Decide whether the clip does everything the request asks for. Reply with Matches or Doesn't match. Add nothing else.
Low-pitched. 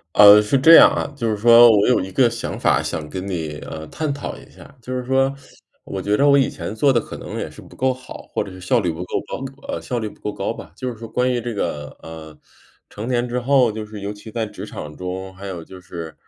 Matches